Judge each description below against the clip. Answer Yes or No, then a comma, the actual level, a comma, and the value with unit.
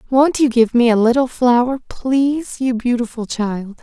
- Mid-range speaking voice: No, high, 245 Hz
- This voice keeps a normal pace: Yes, average, 170 wpm